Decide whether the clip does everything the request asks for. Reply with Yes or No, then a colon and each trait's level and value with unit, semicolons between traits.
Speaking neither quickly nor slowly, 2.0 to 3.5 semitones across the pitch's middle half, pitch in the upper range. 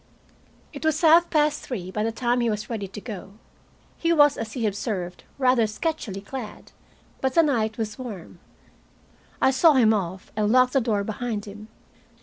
No: average, 175 wpm; average, 4.2 semitones; high, 225 Hz